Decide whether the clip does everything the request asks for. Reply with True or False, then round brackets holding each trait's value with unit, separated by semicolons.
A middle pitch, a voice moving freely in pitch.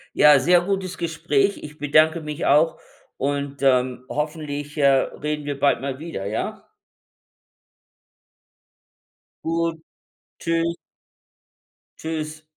False (150 Hz; 2.6 semitones)